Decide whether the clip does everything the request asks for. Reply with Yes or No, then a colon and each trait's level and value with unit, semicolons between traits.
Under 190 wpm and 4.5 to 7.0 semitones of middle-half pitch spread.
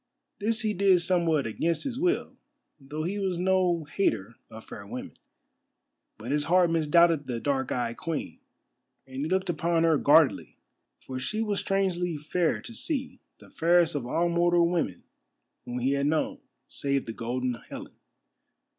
Yes: average, 160 wpm; average, 4.8 semitones